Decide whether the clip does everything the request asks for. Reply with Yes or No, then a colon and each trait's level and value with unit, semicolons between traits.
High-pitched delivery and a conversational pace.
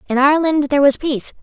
No: very high, 285 Hz; fast, 210 wpm